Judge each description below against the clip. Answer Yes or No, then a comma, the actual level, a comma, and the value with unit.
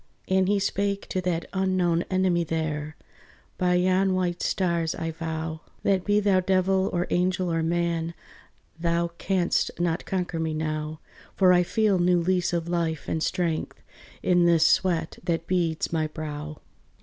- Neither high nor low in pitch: Yes, medium, 175 Hz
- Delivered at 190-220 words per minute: No, average, 155 wpm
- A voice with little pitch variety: Yes, narrow, 2.3 semitones